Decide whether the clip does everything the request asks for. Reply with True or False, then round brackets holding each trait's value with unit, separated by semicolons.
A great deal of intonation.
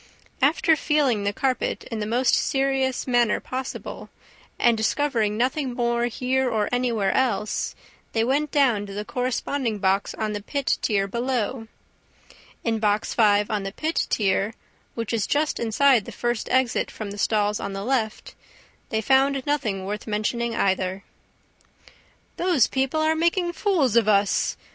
False (4.2 semitones)